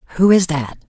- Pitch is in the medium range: Yes, medium, 165 Hz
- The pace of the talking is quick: No, average, 190 wpm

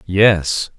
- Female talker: No, male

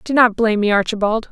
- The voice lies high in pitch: Yes, high, 220 Hz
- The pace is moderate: No, fast, 230 wpm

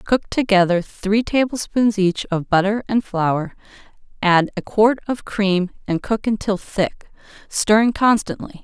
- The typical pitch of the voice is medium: No, high, 205 Hz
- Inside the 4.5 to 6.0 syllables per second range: No, 4.2 syllables/s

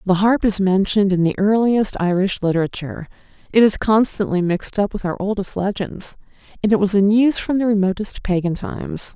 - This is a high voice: Yes, high, 195 Hz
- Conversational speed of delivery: Yes, average, 185 wpm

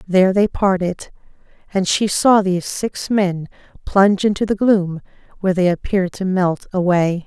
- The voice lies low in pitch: No, high, 190 Hz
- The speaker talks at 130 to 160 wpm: Yes, average, 155 wpm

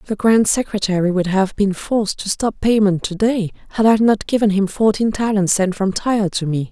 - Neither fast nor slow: No, fast, 215 wpm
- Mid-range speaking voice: No, high, 205 Hz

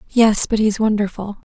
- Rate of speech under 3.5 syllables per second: No, 5.0 syllables/s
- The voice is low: No, high, 210 Hz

